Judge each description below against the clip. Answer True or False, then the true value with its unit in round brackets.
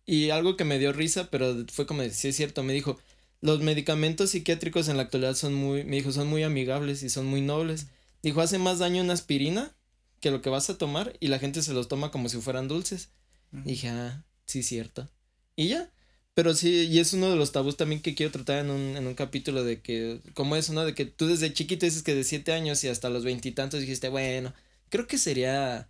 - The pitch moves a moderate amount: True (3.5 semitones)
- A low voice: False (145 Hz)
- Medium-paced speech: False (235 wpm)